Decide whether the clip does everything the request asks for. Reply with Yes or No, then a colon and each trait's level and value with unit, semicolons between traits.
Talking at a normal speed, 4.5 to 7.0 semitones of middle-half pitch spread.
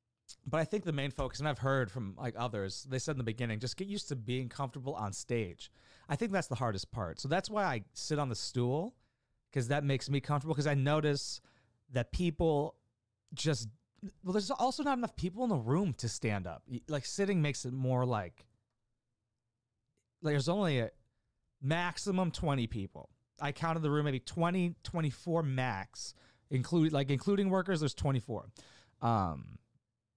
Yes: average, 180 wpm; average, 5.1 semitones